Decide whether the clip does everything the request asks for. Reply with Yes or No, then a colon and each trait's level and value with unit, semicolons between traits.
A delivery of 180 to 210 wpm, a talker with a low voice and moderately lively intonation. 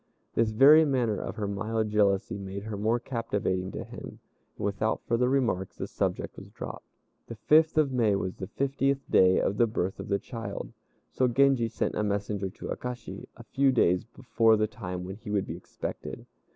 Yes: average, 190 wpm; low, 110 Hz; average, 4.0 semitones